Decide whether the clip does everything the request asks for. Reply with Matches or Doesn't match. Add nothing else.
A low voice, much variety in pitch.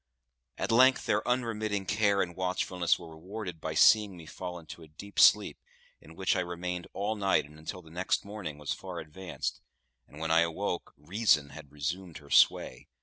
Doesn't match